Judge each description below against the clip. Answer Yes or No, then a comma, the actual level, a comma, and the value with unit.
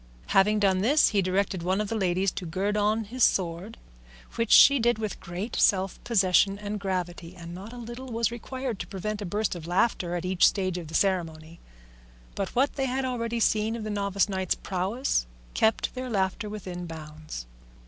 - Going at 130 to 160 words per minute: No, average, 190 wpm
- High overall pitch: Yes, high, 200 Hz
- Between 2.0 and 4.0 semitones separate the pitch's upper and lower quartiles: Yes, average, 3.7 semitones